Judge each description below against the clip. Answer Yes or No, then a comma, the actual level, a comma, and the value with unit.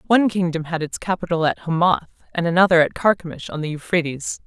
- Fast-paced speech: No, average, 190 wpm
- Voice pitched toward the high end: No, medium, 170 Hz